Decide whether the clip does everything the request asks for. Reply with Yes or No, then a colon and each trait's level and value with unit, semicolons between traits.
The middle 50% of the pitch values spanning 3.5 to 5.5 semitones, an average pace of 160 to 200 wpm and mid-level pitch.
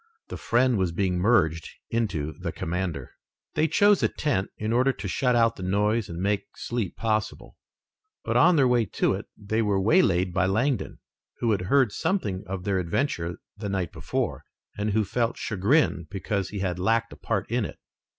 No: average, 4.2 semitones; average, 185 wpm; low, 105 Hz